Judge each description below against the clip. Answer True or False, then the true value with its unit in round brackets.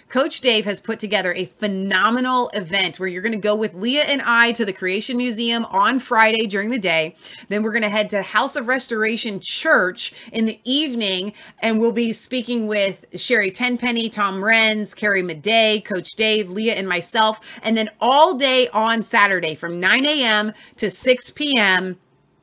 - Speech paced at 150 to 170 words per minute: False (180 wpm)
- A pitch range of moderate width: True (3.4 semitones)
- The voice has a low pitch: False (220 Hz)